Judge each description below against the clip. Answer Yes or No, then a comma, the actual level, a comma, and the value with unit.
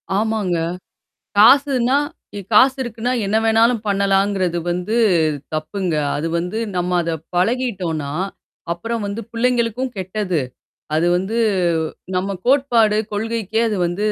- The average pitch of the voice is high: Yes, high, 210 Hz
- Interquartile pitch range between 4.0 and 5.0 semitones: Yes, average, 4.3 semitones